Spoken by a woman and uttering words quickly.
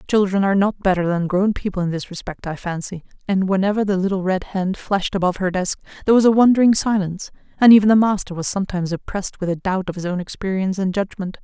Yes: female; fast, 225 wpm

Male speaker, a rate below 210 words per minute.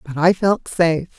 No: female; average, 200 wpm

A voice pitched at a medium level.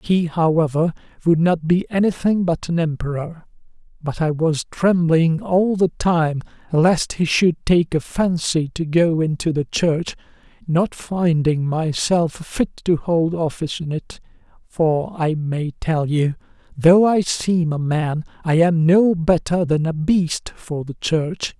Yes: medium, 165 Hz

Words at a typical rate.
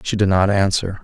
No: fast, 230 wpm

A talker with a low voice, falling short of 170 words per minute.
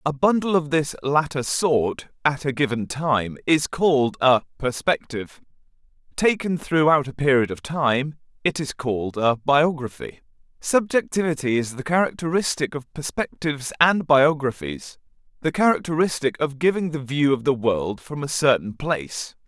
No: medium, 145 Hz; average, 140 wpm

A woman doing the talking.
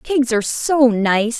Yes: female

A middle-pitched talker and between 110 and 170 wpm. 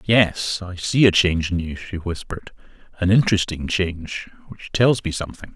No: very low, 90 Hz; average, 160 wpm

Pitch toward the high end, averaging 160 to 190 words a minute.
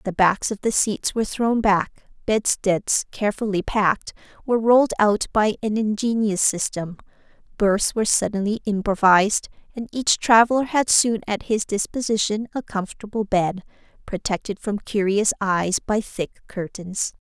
No: high, 210 Hz; average, 140 wpm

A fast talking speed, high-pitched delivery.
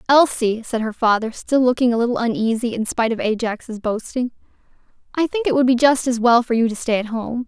Yes: fast, 225 wpm; high, 240 Hz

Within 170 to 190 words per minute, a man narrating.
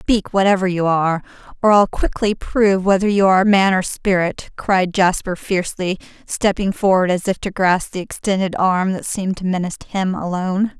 No: average, 180 wpm; female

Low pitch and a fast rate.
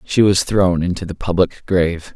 No: very low, 90 Hz; average, 195 wpm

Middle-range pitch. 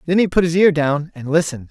Yes: medium, 160 Hz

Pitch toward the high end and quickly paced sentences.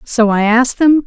Yes: high, 245 Hz; fast, 225 wpm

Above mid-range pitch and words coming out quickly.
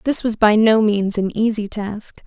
Yes: high, 215 Hz; fast, 210 wpm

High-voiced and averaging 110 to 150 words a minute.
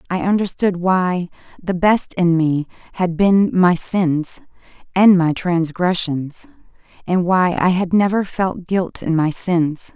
No: medium, 180 Hz; average, 145 wpm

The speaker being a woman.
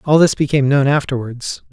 No: male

